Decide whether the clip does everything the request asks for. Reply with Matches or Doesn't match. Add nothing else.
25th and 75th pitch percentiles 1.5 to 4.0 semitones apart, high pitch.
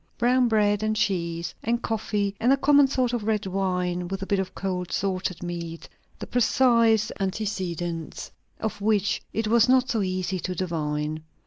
Matches